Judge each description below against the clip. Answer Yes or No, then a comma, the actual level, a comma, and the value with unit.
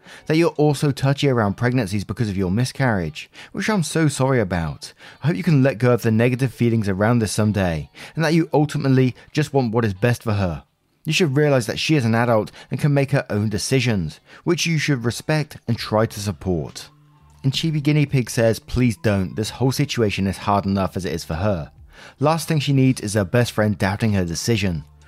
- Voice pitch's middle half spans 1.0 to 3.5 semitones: No, wide, 5.5 semitones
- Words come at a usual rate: No, fast, 215 wpm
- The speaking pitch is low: Yes, low, 120 Hz